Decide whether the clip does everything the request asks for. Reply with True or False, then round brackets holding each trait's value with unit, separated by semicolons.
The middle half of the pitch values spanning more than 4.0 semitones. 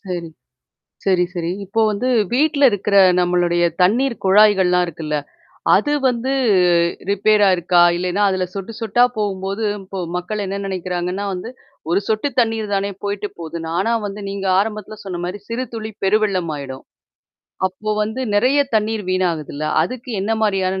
False (3.2 semitones)